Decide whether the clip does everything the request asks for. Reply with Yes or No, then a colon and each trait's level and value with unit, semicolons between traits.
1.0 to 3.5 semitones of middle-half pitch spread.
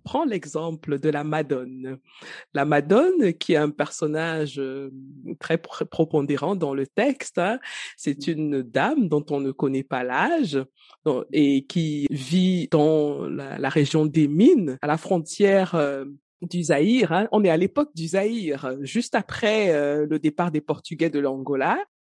No: average, 4.0 semitones